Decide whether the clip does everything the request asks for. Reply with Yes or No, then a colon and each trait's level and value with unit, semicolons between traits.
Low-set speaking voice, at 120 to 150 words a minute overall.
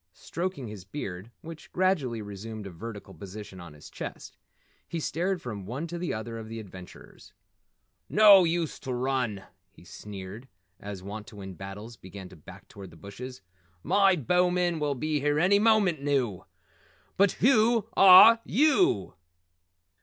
Yes: low, 125 Hz; average, 145 wpm